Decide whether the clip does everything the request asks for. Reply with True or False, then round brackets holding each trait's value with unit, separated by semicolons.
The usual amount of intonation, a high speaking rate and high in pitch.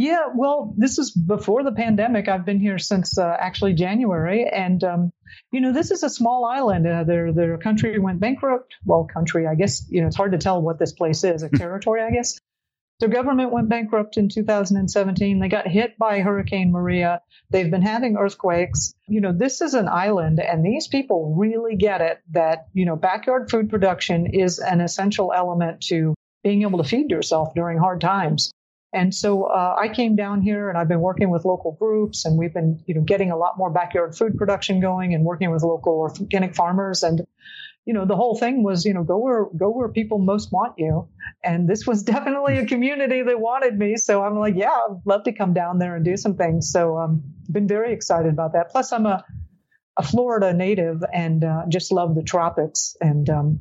True (4.2 semitones; 210 wpm; 195 Hz)